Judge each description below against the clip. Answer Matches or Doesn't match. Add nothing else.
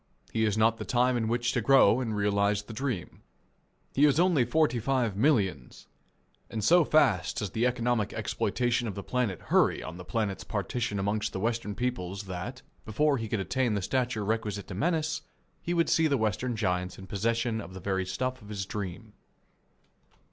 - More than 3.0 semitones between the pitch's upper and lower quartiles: Matches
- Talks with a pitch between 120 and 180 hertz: Doesn't match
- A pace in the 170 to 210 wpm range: Matches